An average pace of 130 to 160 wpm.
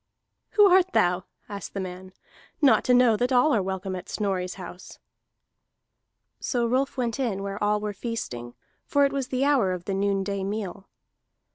No: average, 170 wpm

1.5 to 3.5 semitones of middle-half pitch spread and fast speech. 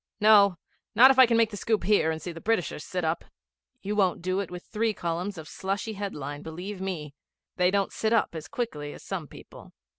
No: average, 4.1 semitones; fast, 215 wpm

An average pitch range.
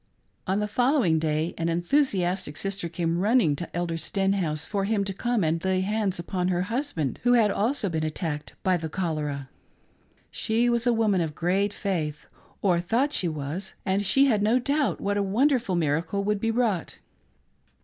Yes: average, 4.9 semitones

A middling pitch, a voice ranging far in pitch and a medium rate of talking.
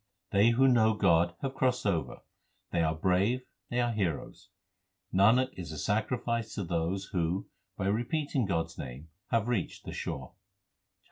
No: low, 100 Hz; wide, 5.8 semitones; average, 155 wpm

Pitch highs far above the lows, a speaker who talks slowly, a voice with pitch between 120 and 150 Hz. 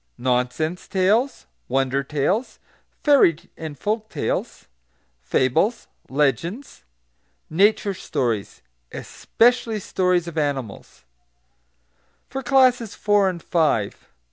No: wide, 8.1 semitones; slow, 90 wpm; medium, 170 Hz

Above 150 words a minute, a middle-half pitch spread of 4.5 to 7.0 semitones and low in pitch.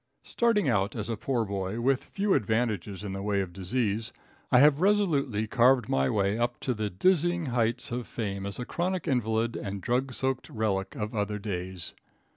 Yes: average, 185 wpm; average, 4.8 semitones; low, 115 Hz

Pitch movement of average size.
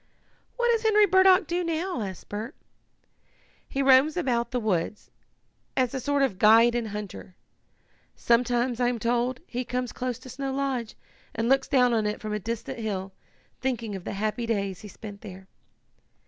Yes: average, 4.0 semitones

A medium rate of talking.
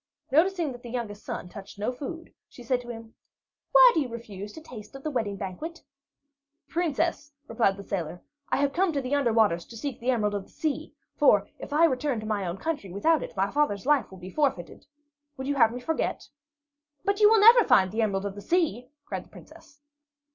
No: fast, 220 wpm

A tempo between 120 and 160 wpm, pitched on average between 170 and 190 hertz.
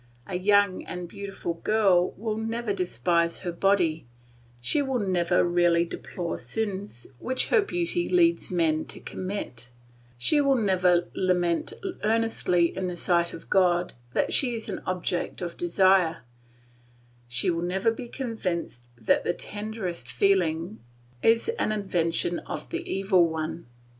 Yes: average, 140 wpm; medium, 185 Hz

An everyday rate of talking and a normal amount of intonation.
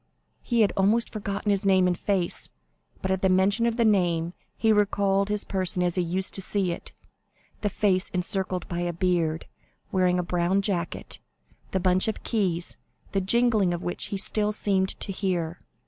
No: average, 180 wpm; narrow, 2.2 semitones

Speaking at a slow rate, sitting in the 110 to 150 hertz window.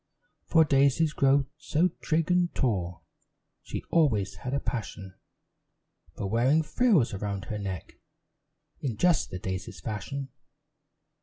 Yes: slow, 125 wpm; low, 135 Hz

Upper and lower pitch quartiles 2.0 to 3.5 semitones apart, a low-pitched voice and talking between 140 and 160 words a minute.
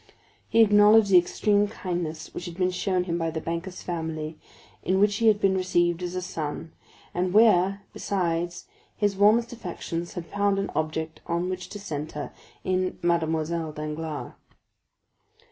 No: average, 3.2 semitones; medium, 180 Hz; average, 155 wpm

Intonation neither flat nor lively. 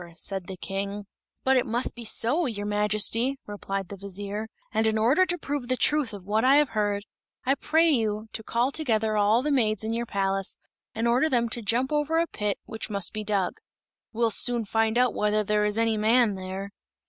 Yes: average, 3.3 semitones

